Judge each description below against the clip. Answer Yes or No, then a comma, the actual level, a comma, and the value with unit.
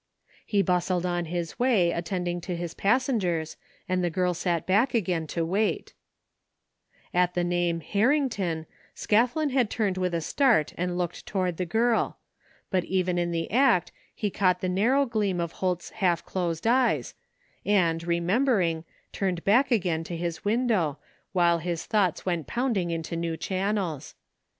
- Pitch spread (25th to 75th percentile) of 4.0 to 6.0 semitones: No, average, 3.6 semitones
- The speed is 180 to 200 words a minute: No, average, 160 wpm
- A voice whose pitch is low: No, medium, 180 Hz